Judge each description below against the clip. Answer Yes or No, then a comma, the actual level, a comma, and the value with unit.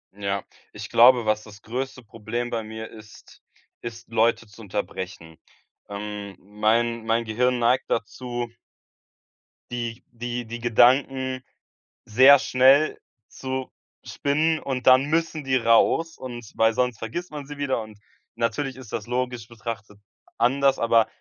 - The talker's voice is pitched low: Yes, low, 120 Hz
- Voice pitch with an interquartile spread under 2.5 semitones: No, average, 2.8 semitones